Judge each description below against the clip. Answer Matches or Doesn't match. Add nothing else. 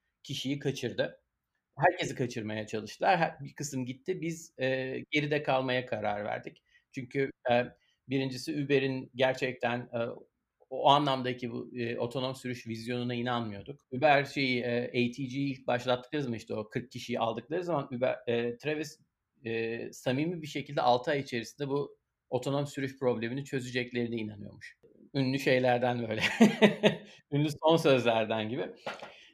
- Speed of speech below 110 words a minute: Doesn't match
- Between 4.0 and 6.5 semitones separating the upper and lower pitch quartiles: Doesn't match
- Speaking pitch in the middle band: Doesn't match